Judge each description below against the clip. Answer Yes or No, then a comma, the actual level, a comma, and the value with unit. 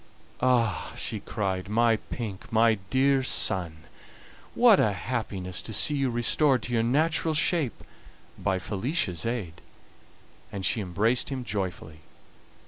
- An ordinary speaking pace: No, slow, 130 wpm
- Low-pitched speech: Yes, low, 115 Hz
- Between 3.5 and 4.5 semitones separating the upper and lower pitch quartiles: No, wide, 5.5 semitones